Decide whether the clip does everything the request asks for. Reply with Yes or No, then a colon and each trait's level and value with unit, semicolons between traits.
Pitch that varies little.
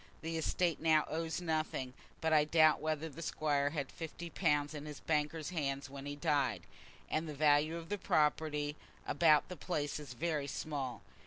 Yes: narrow, 1.9 semitones